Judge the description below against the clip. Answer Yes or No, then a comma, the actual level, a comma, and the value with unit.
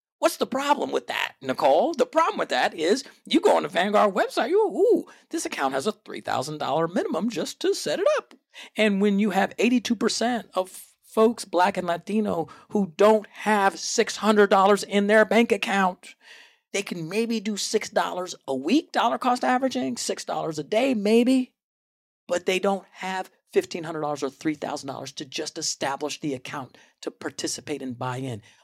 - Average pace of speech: Yes, average, 165 wpm